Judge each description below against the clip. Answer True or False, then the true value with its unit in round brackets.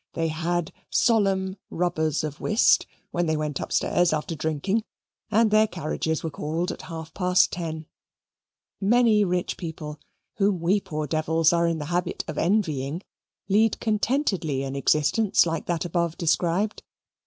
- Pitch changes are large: False (3.7 semitones)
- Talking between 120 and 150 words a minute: True (145 wpm)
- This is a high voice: False (170 Hz)